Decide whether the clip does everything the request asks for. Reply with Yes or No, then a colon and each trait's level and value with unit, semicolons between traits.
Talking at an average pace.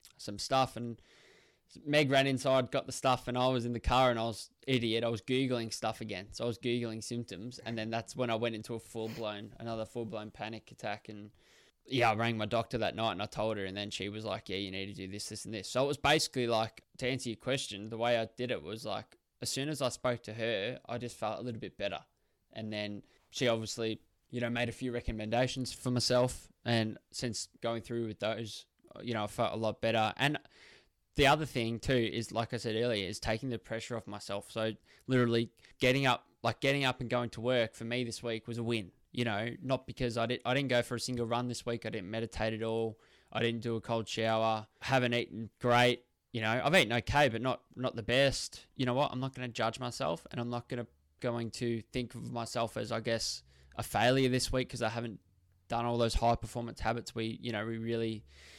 No: fast, 245 wpm